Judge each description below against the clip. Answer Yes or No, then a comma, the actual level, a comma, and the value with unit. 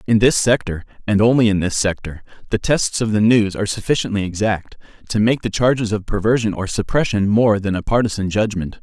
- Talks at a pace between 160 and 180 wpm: No, average, 195 wpm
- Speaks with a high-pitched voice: No, low, 105 Hz